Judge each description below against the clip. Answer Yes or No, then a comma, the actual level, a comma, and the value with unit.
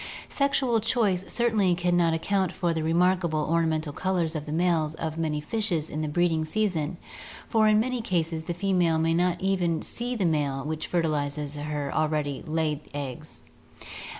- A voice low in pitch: No, medium, 165 Hz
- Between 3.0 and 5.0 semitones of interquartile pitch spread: Yes, average, 3.3 semitones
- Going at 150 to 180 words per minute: Yes, average, 170 wpm